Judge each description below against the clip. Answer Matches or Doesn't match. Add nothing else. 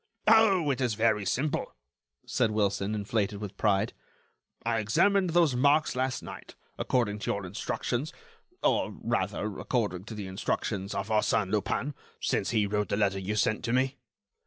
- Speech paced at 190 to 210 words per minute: Doesn't match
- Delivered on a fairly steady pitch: Doesn't match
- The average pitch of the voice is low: Matches